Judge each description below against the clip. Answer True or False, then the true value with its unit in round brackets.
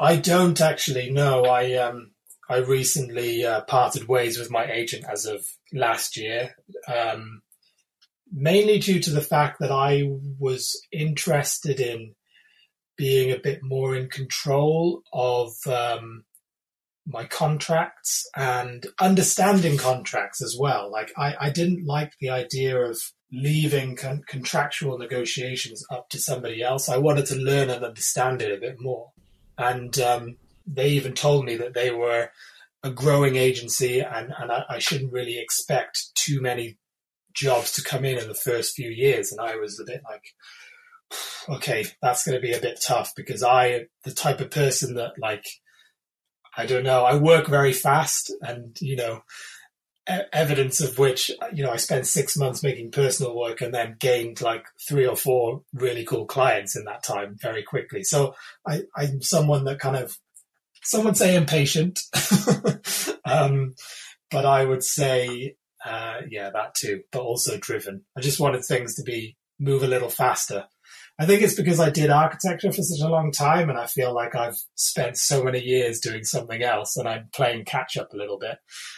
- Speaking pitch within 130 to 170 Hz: True (135 Hz)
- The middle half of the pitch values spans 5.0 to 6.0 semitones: False (3.4 semitones)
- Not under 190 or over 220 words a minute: False (170 wpm)